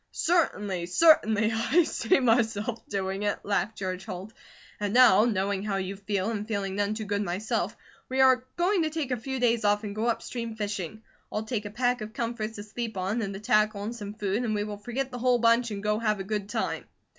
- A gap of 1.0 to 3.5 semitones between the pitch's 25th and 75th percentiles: Yes, average, 2.8 semitones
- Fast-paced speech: Yes, fast, 220 wpm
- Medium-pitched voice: No, high, 215 Hz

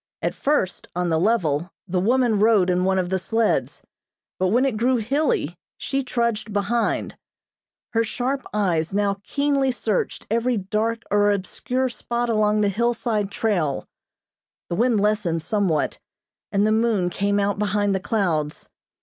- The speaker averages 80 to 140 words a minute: No, average, 150 wpm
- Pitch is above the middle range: Yes, high, 210 Hz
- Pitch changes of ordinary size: Yes, average, 3.8 semitones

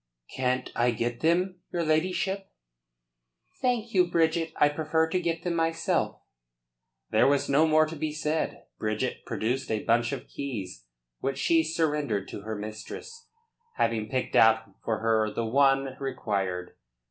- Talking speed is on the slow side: No, average, 145 wpm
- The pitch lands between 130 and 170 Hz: Yes, medium, 140 Hz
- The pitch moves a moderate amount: No, wide, 6.5 semitones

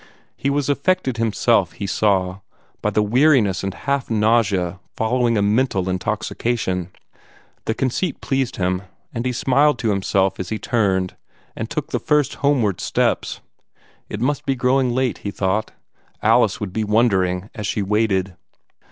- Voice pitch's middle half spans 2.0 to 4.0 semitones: No, average, 4.8 semitones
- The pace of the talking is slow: No, average, 150 wpm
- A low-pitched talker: Yes, low, 110 Hz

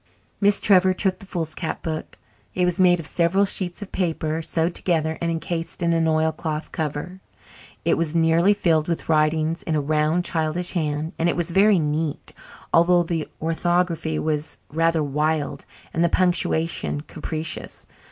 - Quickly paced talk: No, average, 160 wpm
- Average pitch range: No, narrow, 2.1 semitones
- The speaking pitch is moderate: Yes, medium, 165 Hz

